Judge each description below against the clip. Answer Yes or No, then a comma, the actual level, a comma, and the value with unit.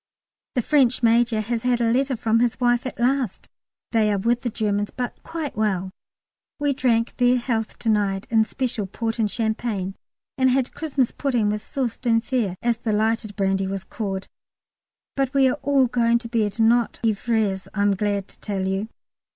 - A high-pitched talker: Yes, high, 230 Hz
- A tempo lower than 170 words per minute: No, average, 180 wpm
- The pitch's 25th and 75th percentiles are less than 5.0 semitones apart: Yes, average, 3.0 semitones